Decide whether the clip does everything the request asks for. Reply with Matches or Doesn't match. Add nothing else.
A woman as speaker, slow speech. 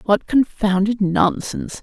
Matches